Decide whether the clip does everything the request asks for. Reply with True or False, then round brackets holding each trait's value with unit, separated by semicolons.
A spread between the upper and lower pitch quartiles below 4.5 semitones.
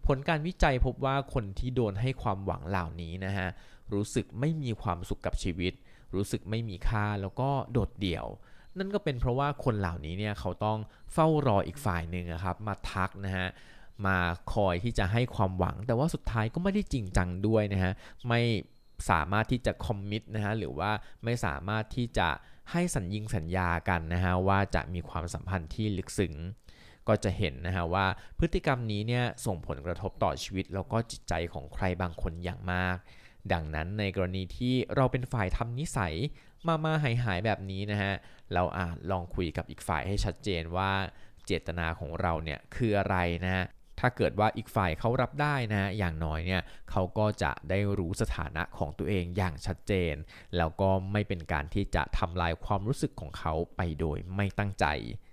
True (4.0 semitones)